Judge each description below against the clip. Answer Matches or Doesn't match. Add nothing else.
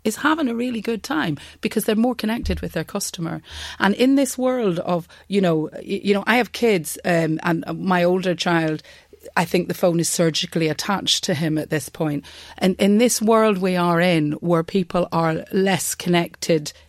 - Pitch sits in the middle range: Matches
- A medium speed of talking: Matches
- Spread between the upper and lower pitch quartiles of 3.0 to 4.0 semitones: Doesn't match